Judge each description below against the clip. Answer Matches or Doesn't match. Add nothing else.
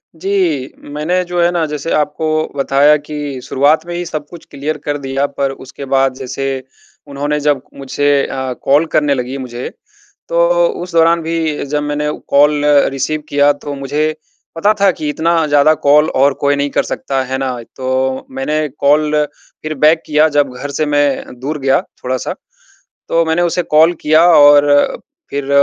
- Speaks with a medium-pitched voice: Matches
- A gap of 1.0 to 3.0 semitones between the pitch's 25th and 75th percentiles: Matches